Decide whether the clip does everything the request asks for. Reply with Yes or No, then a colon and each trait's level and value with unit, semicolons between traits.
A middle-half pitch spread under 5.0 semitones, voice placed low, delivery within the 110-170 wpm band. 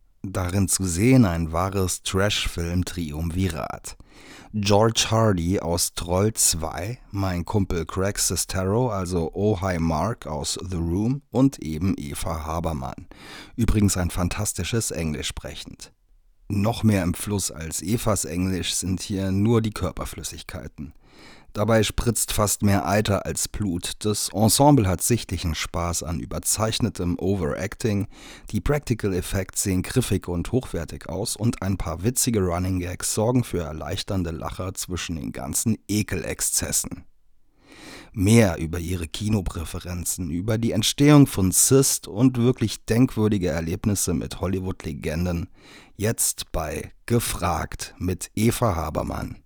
Yes: average, 3.9 semitones; very low, 95 Hz; slow, 125 wpm